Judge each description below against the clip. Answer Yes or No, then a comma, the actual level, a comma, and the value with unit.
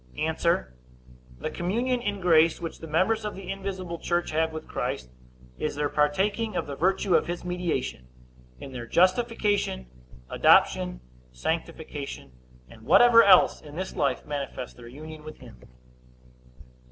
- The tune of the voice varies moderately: No, wide, 5.9 semitones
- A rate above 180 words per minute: No, average, 140 wpm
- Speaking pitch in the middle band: Yes, medium, 160 Hz